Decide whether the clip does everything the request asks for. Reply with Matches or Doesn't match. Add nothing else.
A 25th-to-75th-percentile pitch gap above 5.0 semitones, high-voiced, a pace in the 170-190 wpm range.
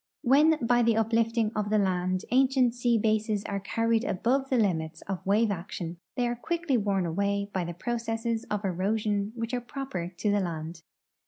Doesn't match